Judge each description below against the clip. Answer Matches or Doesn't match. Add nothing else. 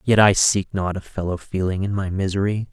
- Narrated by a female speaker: Doesn't match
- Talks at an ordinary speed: Doesn't match